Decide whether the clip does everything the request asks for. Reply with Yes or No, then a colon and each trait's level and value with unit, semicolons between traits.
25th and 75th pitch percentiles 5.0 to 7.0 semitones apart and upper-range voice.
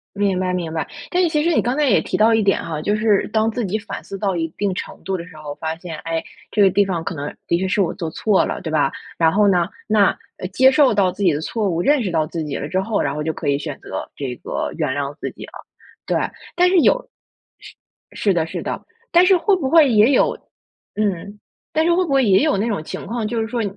Yes: wide, 5.6 semitones; high, 195 Hz